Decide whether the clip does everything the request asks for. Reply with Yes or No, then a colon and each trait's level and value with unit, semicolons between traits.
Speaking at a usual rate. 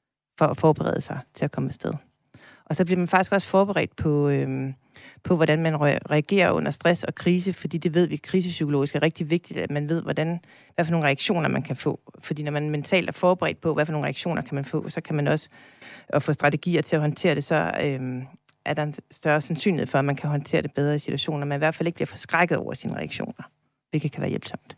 No: fast, 240 wpm